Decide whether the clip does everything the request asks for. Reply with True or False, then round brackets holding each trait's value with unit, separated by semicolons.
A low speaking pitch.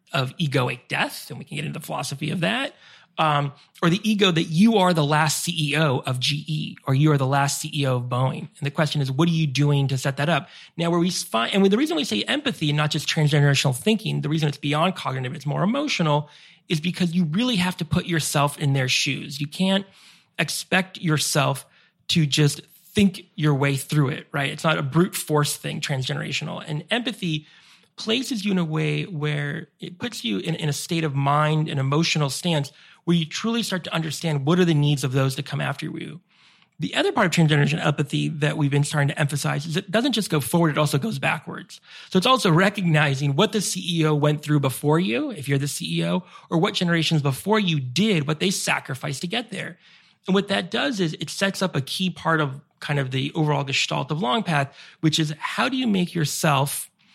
False (155 Hz)